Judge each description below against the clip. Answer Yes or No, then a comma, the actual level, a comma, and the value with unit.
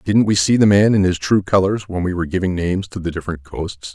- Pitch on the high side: No, very low, 95 Hz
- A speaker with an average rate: No, fast, 275 wpm